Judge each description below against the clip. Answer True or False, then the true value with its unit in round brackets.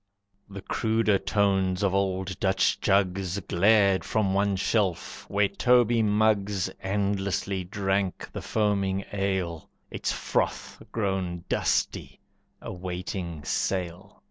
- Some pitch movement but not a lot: False (1.5 semitones)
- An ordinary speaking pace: False (105 wpm)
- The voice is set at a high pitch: False (95 Hz)